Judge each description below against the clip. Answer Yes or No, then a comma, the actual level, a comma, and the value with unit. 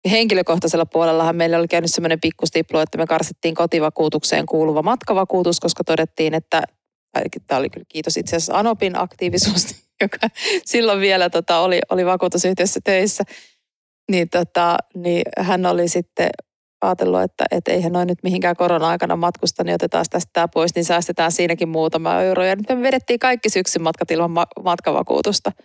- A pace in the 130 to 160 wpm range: Yes, average, 150 wpm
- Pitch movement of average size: No, narrow, 2.1 semitones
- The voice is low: No, medium, 175 Hz